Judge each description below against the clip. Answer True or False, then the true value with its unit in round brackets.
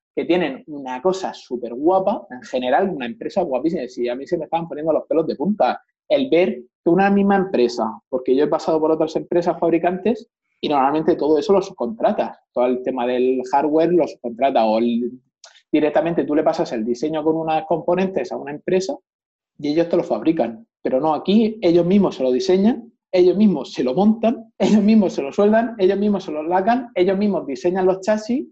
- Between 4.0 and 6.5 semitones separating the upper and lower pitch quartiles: True (5.3 semitones)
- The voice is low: False (175 Hz)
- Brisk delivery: True (200 wpm)